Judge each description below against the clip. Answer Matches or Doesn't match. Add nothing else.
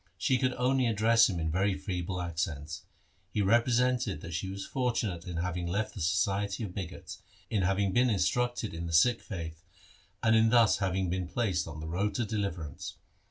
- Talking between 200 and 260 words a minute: Doesn't match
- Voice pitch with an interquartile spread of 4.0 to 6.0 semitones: Matches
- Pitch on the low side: Matches